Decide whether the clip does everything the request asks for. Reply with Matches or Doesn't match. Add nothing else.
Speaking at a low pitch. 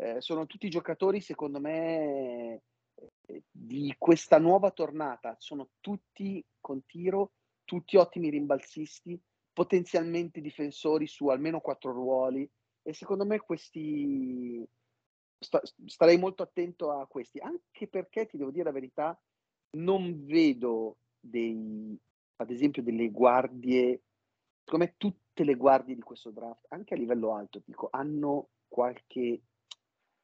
Doesn't match